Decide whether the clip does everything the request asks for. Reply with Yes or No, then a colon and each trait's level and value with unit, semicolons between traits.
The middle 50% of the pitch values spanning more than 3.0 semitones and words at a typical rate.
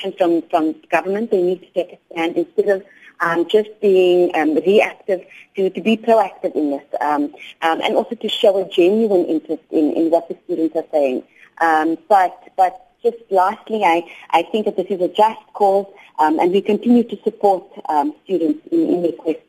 Yes: average, 4.0 semitones; average, 190 wpm